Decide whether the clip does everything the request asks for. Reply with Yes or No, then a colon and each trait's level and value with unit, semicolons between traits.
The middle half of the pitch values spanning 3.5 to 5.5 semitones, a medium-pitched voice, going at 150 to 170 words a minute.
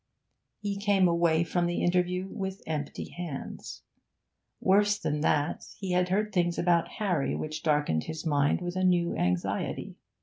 No: average, 3.0 semitones; medium, 175 Hz; average, 155 wpm